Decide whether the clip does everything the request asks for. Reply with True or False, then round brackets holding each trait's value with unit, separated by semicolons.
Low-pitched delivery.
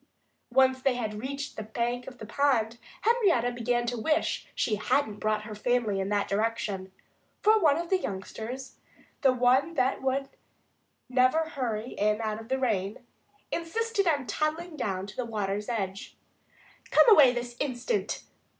False (245 Hz)